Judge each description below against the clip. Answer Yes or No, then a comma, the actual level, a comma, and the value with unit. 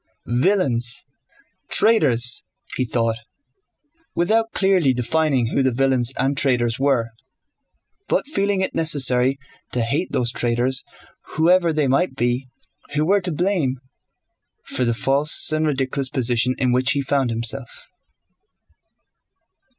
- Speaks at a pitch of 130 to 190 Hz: Yes, low, 135 Hz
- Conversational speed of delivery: No, slow, 120 wpm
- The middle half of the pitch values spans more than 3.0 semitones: Yes, average, 4.4 semitones